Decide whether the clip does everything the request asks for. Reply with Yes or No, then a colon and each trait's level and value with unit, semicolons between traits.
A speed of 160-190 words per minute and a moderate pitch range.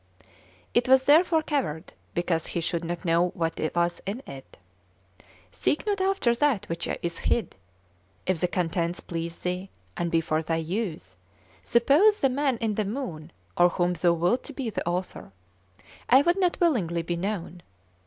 No: average, 165 wpm; wide, 7.5 semitones